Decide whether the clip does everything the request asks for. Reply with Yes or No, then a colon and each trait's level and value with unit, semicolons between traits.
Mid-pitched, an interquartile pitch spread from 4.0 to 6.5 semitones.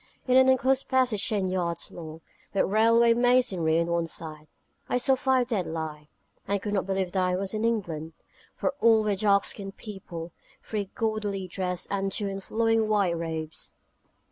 No: high, 200 Hz; average, 4.7 semitones